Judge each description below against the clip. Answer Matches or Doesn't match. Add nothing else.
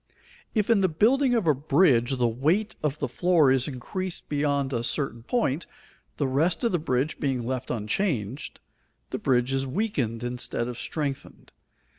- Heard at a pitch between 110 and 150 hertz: Matches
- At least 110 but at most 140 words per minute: Doesn't match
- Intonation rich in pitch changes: Matches